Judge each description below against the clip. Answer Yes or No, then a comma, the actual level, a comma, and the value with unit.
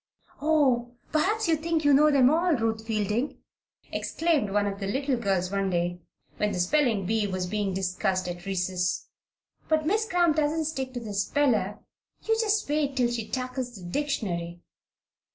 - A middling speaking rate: Yes, average, 170 wpm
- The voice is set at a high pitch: Yes, high, 240 Hz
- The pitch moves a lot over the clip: Yes, wide, 7.4 semitones